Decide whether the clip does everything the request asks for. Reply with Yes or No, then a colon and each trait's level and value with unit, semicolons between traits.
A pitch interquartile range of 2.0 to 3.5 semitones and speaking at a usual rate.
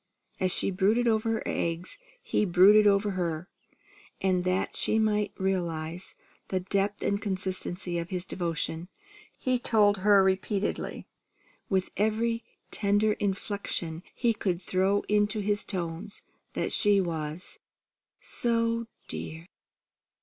No: narrow, 2.6 semitones; slow, 120 wpm